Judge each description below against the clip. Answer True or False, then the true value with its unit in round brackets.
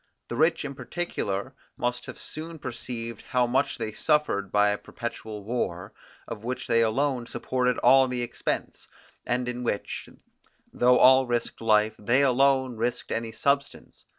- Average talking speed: True (150 wpm)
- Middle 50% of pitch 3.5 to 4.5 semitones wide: False (2.7 semitones)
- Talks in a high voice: False (125 Hz)